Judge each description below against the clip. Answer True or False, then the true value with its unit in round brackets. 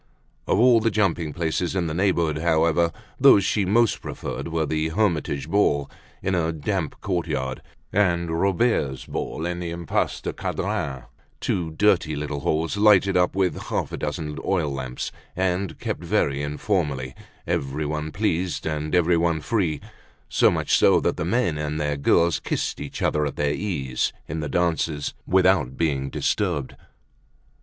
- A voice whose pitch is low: True (80 Hz)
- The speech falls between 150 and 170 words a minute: True (155 wpm)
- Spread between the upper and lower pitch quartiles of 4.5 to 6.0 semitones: False (3.8 semitones)